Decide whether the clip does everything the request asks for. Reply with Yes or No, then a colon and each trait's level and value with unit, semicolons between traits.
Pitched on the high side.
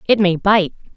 Yes: high, 195 Hz